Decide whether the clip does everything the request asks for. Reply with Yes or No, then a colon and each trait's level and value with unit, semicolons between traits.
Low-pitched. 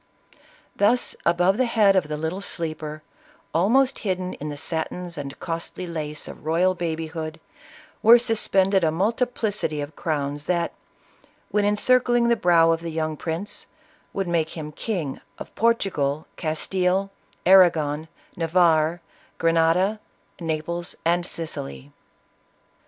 No: medium, 170 Hz